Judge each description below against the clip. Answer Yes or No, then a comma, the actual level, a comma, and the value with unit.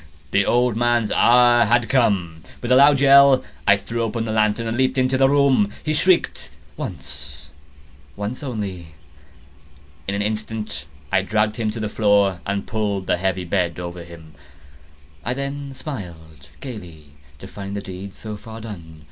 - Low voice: Yes, low, 105 Hz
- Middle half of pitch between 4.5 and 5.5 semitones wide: Yes, average, 5.2 semitones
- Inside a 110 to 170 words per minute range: Yes, average, 160 wpm